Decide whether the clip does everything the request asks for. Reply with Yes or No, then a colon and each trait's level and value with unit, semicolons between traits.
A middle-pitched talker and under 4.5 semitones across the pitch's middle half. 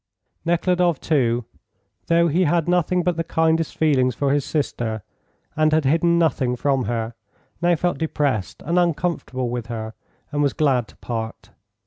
No: medium, 150 Hz; average, 5.3 semitones